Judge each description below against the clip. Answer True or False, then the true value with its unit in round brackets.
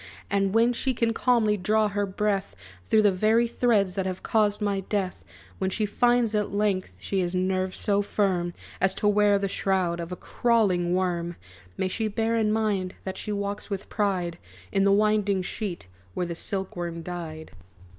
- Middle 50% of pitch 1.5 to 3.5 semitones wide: True (2.4 semitones)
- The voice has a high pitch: True (200 Hz)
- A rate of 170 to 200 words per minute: True (185 wpm)